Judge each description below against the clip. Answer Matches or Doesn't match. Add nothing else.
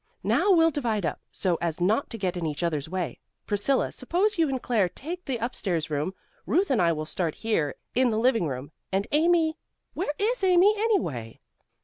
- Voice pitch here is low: Doesn't match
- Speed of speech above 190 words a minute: Matches